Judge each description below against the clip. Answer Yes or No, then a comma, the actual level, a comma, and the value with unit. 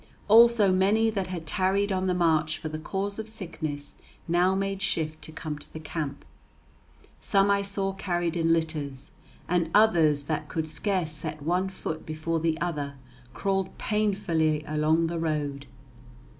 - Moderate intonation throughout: Yes, average, 3.8 semitones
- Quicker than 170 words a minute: No, average, 155 wpm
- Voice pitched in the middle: Yes, medium, 165 Hz